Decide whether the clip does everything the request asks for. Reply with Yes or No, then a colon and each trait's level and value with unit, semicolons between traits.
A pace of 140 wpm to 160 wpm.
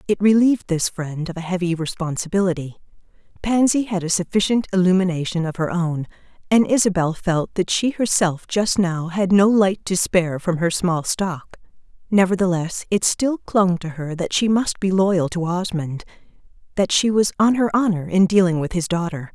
No: average, 175 wpm